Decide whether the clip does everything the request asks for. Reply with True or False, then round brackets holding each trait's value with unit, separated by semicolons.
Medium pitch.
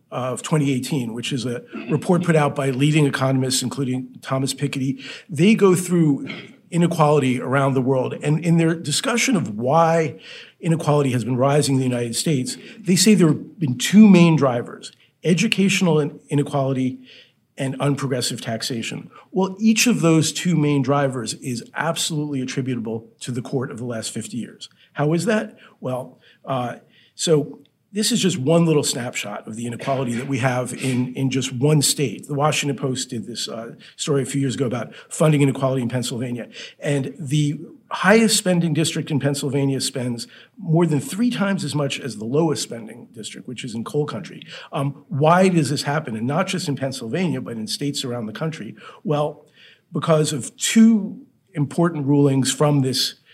True (145 Hz)